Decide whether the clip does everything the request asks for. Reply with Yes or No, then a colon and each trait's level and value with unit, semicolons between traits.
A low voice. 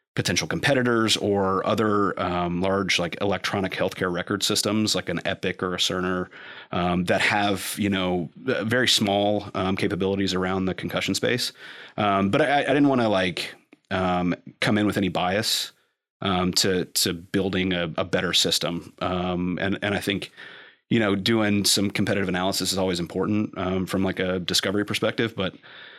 Yes: very low, 95 Hz